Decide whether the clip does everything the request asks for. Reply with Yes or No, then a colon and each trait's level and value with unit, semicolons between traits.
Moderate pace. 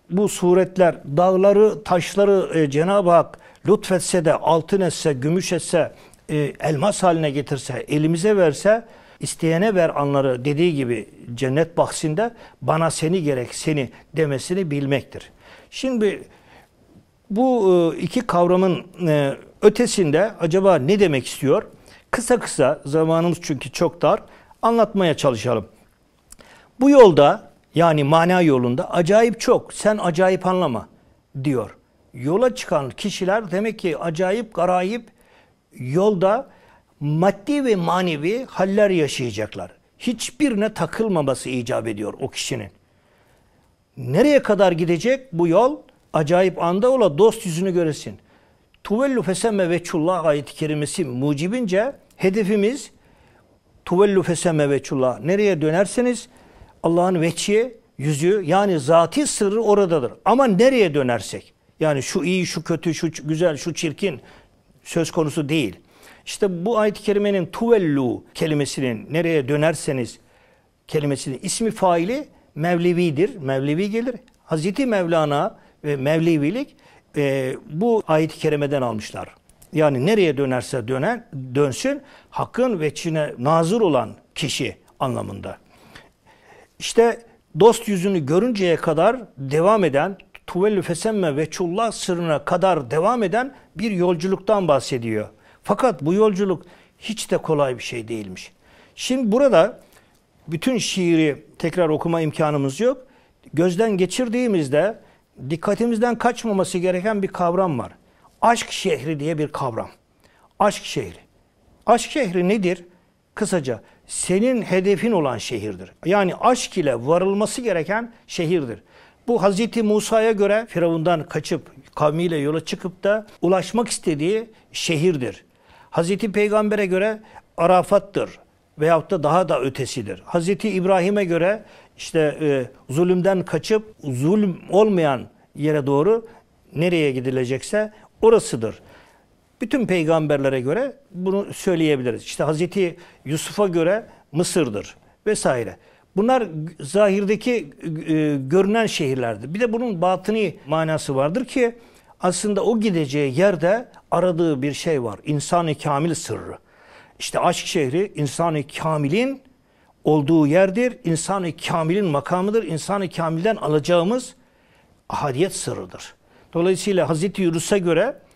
Yes: average, 110 wpm